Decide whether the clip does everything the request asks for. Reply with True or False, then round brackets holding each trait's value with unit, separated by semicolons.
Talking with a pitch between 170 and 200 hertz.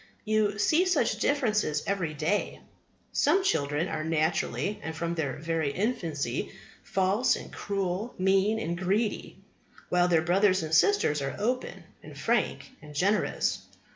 True (185 Hz)